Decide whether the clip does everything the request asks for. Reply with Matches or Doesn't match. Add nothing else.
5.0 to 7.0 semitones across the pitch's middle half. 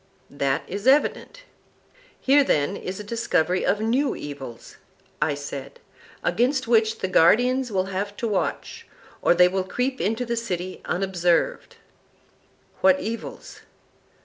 Matches